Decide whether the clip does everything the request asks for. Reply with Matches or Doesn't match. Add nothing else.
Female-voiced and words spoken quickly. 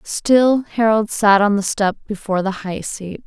Doesn't match